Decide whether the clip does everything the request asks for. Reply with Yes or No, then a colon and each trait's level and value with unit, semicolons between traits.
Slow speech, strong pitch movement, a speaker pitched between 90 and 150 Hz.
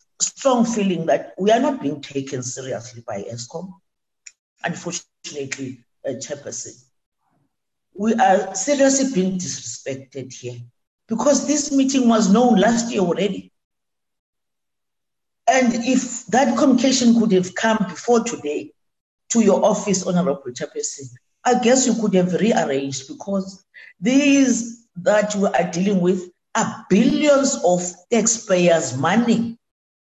No: slow, 120 wpm; wide, 6.2 semitones; high, 200 Hz